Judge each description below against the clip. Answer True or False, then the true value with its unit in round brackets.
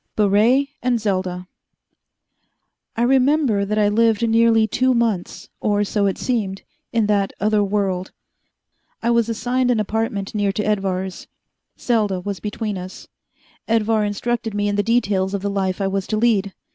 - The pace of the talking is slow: False (160 wpm)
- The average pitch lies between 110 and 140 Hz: False (210 Hz)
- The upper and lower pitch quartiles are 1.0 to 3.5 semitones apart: True (2.6 semitones)